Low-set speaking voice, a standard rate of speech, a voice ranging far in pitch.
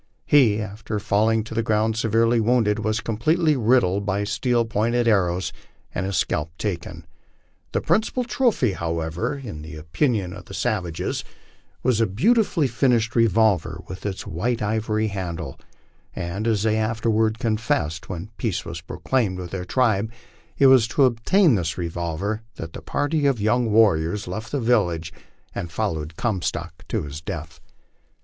No: low, 110 Hz; average, 155 wpm; average, 4.9 semitones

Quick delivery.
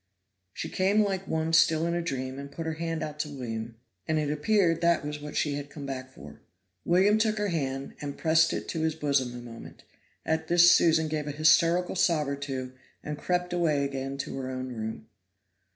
Yes: fast, 210 wpm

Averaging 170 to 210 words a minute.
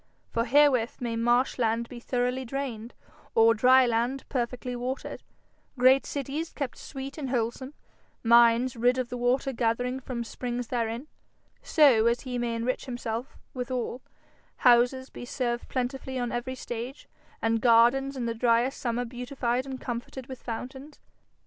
No: average, 150 wpm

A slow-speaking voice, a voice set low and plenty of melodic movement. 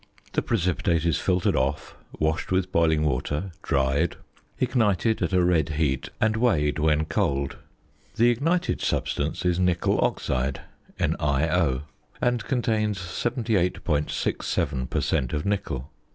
Yes: slow, 125 wpm; very low, 85 Hz; wide, 6.0 semitones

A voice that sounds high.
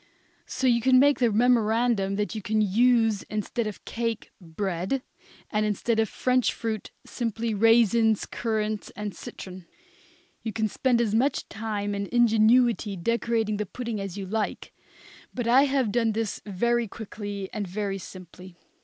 Yes: high, 220 Hz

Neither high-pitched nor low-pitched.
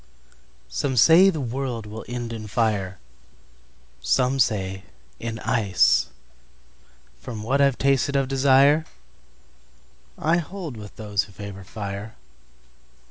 No: low, 110 Hz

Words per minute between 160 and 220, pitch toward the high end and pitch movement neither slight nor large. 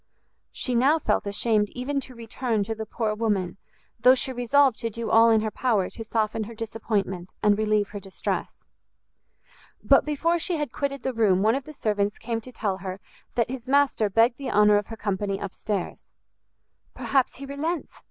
Yes: average, 190 wpm; high, 225 Hz; average, 3.8 semitones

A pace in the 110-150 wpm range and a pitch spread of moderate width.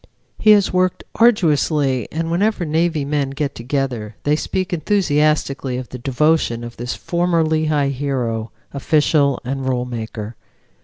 Yes: average, 140 wpm; average, 4.3 semitones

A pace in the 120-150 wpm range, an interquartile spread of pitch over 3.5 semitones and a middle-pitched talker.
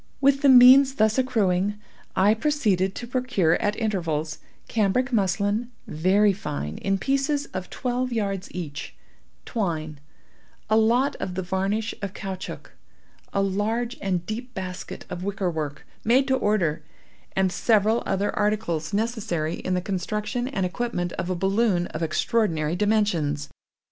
No: average, 140 wpm; average, 4.4 semitones; high, 200 Hz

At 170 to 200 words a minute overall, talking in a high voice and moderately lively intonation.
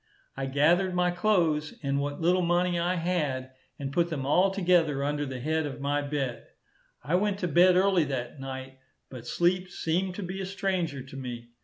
No: average, 190 wpm; medium, 160 Hz; average, 4.6 semitones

